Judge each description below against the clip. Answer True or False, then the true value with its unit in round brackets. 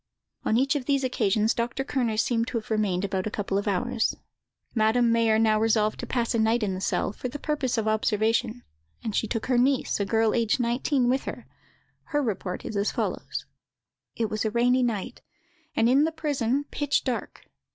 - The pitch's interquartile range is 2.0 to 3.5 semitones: True (2.8 semitones)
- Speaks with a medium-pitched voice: False (230 Hz)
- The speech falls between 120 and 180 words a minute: False (200 wpm)